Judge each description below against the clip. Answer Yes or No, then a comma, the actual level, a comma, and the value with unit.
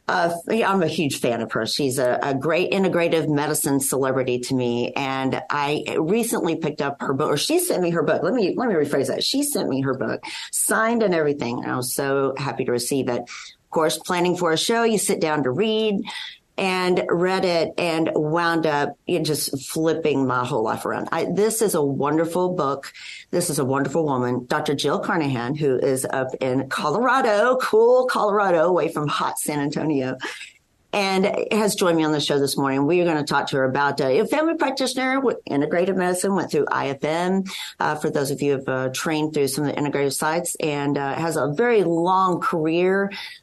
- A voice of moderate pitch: Yes, medium, 155 Hz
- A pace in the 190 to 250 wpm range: Yes, fast, 205 wpm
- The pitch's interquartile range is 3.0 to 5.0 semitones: Yes, average, 4.6 semitones